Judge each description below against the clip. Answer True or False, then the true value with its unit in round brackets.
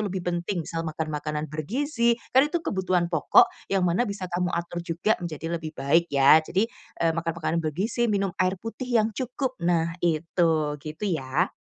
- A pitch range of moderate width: True (4.0 semitones)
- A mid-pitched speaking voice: True (175 Hz)